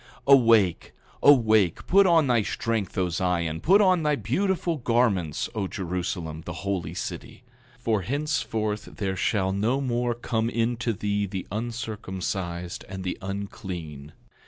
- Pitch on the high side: No, low, 105 Hz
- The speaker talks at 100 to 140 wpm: Yes, slow, 135 wpm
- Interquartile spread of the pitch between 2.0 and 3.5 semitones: No, average, 4.7 semitones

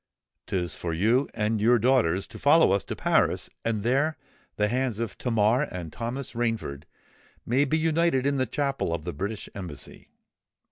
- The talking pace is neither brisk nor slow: Yes, average, 170 wpm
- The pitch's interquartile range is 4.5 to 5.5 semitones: Yes, average, 5.1 semitones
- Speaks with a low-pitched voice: Yes, low, 115 Hz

